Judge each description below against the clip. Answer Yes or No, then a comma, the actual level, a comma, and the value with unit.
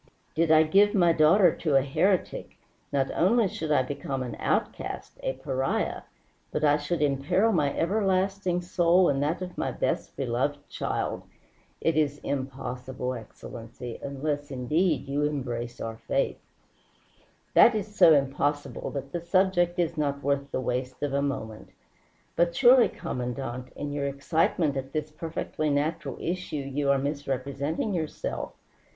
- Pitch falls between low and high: Yes, medium, 145 Hz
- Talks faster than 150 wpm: No, average, 145 wpm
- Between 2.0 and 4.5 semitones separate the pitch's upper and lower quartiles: Yes, average, 4.0 semitones